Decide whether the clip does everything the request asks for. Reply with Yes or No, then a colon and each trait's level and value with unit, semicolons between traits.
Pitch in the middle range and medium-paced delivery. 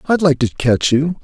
No: medium, 145 Hz; fast, 245 wpm